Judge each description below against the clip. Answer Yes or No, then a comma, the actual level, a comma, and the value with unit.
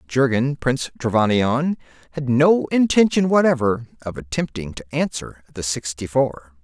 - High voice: No, low, 130 Hz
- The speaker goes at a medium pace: No, slow, 120 wpm